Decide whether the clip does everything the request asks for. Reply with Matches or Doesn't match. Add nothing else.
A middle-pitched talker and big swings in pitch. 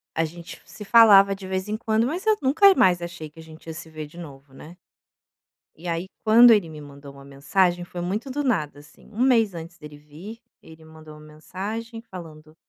Matches